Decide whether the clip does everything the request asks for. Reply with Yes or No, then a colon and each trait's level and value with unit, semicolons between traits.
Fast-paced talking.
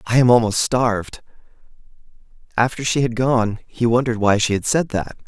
No: average, 170 wpm